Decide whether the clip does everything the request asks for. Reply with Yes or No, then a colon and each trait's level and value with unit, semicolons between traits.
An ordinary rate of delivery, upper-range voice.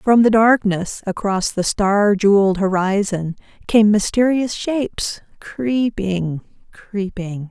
No: slow, 105 wpm; high, 205 Hz